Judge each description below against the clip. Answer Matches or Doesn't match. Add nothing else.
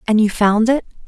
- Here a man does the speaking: Doesn't match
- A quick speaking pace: Matches